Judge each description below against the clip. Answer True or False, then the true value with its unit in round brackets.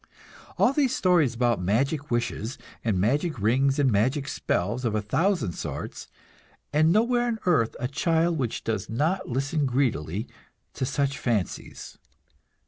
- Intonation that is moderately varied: False (6.0 semitones)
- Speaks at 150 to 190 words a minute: False (140 wpm)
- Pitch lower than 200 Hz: True (135 Hz)